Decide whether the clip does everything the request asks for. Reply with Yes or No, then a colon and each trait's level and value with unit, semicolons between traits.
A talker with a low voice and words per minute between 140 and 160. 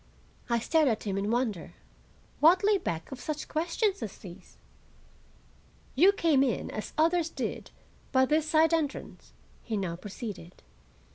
No: very high, 275 Hz; average, 145 wpm